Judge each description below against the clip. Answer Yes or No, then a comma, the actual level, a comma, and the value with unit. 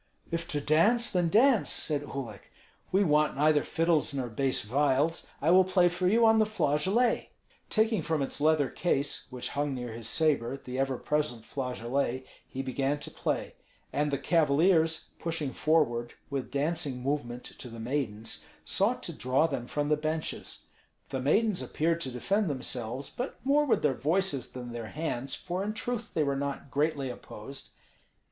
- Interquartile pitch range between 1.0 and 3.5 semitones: No, average, 4.3 semitones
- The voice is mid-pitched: Yes, medium, 145 Hz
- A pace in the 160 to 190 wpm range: Yes, average, 170 wpm